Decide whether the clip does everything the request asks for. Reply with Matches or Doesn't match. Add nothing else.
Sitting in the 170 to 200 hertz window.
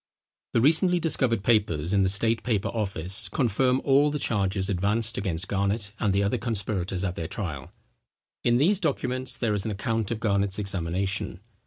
Doesn't match